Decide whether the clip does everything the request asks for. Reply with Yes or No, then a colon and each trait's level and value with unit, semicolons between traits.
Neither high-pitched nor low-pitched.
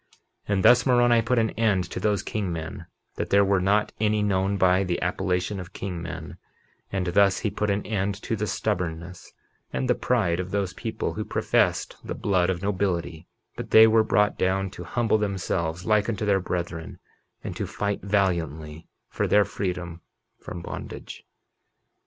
No: very low, 95 Hz